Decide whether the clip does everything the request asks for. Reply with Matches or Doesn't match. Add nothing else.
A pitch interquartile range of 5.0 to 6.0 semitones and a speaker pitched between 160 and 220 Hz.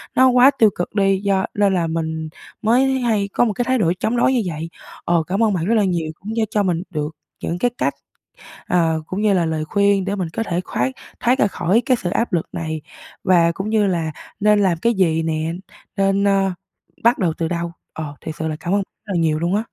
Doesn't match